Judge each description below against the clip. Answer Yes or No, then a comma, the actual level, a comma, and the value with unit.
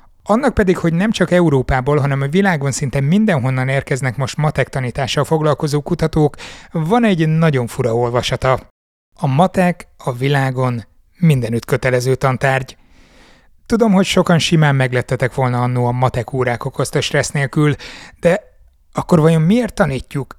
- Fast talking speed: No, average, 140 wpm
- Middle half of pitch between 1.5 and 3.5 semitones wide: No, average, 4.4 semitones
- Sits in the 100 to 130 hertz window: No, medium, 140 Hz